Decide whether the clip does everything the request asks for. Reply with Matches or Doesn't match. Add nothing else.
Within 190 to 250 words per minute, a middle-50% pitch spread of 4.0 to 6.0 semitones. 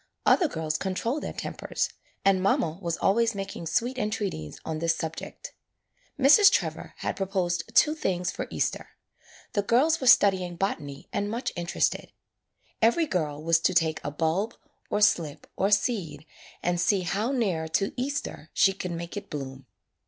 Doesn't match